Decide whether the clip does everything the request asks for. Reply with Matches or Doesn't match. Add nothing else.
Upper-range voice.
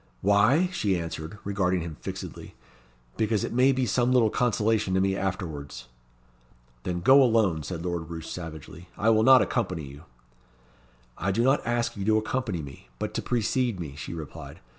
Doesn't match